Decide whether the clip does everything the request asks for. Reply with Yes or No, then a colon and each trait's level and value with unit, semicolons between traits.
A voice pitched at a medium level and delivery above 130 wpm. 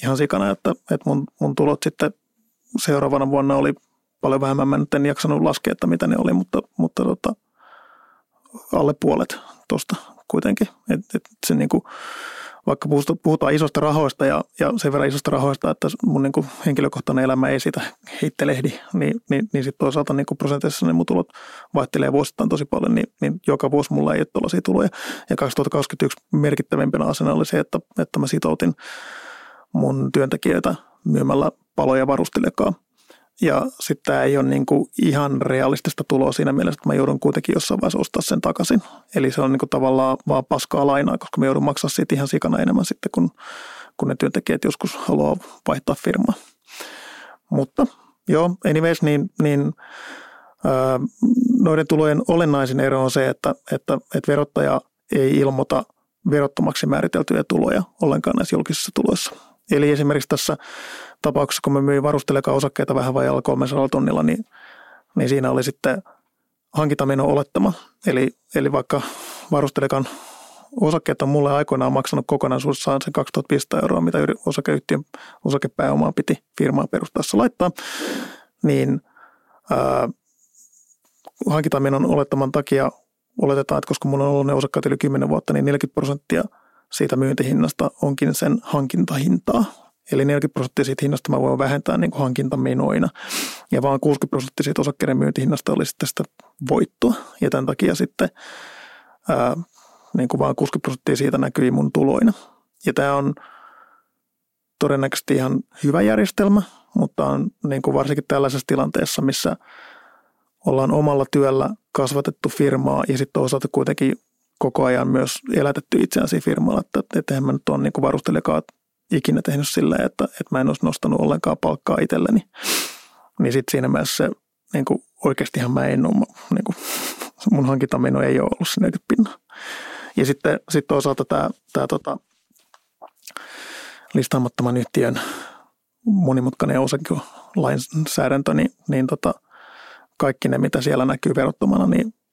Yes: medium, 145 Hz; average, 145 wpm